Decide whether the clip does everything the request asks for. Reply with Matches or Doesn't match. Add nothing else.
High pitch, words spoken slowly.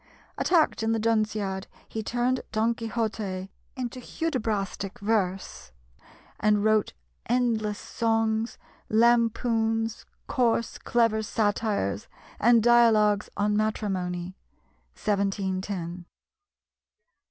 Matches